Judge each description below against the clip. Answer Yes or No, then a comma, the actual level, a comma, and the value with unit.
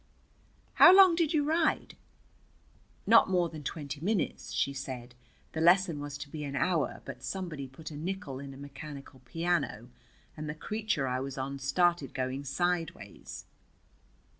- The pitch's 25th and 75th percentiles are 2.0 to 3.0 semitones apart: No, average, 4.7 semitones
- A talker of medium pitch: Yes, medium, 150 Hz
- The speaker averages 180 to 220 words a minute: No, average, 155 wpm